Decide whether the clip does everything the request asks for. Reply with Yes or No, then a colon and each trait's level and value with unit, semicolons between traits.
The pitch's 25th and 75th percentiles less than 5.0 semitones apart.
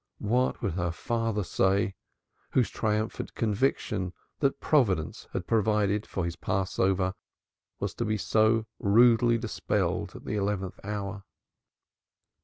Yes: average, 2.9 semitones